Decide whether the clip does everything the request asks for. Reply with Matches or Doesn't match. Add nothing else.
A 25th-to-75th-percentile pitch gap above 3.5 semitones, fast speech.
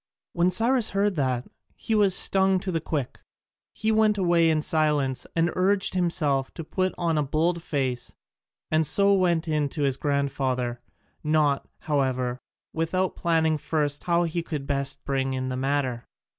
Doesn't match